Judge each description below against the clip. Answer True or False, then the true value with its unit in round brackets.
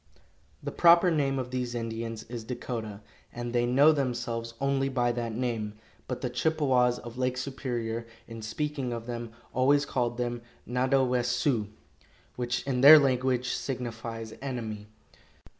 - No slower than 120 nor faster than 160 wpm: True (140 wpm)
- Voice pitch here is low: True (125 Hz)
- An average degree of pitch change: False (2.2 semitones)